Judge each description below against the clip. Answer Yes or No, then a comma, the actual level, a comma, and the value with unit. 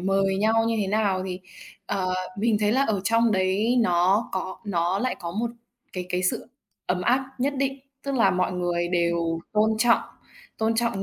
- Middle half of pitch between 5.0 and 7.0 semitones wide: No, average, 3.9 semitones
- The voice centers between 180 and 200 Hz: Yes, high, 195 Hz